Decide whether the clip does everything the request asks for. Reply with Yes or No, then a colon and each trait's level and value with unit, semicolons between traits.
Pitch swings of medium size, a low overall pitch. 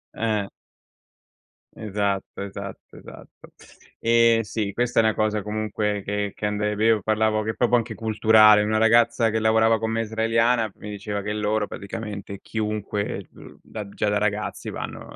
No: narrow, 1.3 semitones; low, 110 Hz